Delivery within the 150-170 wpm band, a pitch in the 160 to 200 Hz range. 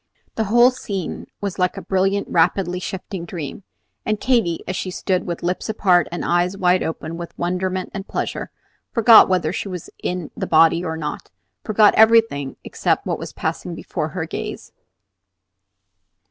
Yes: average, 160 wpm; medium, 185 Hz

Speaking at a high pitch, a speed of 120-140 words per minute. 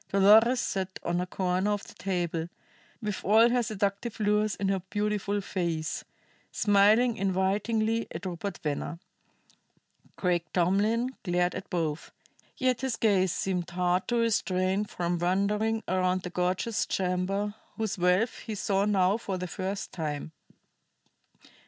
Yes: high, 195 Hz; slow, 135 wpm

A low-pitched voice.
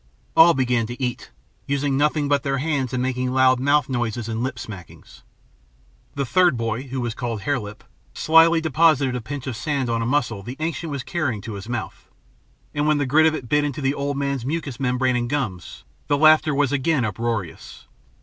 Yes: low, 130 Hz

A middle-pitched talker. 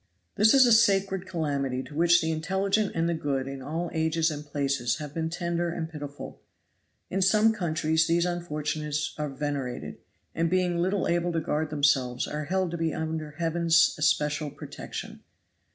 Yes: medium, 160 Hz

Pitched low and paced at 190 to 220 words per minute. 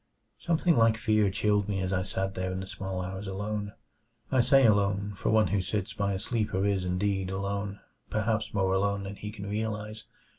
Yes: low, 100 Hz; average, 195 wpm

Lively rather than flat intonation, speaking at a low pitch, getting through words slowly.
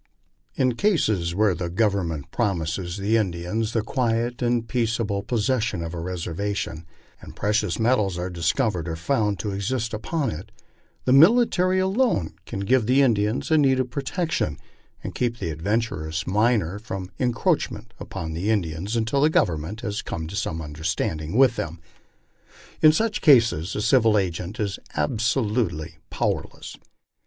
No: wide, 6.0 semitones; low, 105 Hz; average, 145 wpm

